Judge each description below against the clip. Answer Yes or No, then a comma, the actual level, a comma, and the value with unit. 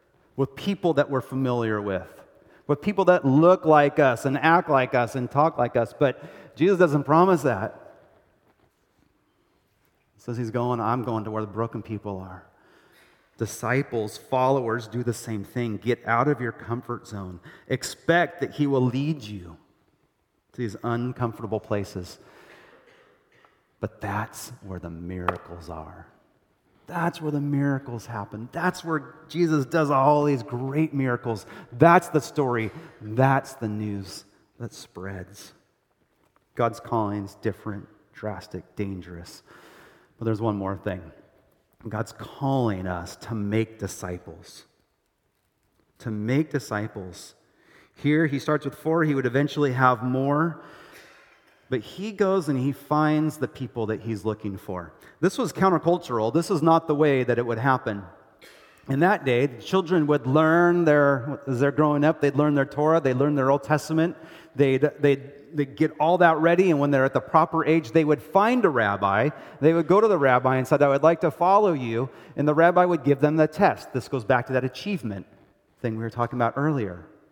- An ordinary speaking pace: Yes, average, 165 wpm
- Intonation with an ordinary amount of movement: No, wide, 5.8 semitones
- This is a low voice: Yes, low, 130 Hz